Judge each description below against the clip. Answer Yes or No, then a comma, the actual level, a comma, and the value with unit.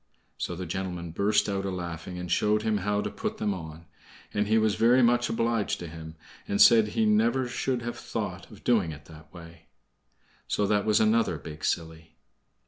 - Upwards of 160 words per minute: Yes, average, 195 wpm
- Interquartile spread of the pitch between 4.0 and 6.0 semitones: Yes, average, 4.7 semitones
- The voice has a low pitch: Yes, low, 100 Hz